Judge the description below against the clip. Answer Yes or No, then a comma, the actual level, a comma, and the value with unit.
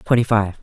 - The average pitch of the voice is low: Yes, low, 110 Hz